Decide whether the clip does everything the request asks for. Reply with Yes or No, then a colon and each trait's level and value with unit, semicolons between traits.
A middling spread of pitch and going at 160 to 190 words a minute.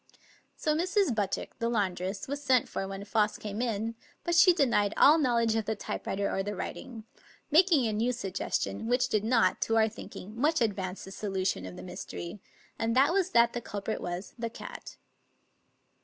Yes: average, 4.1 semitones; average, 185 wpm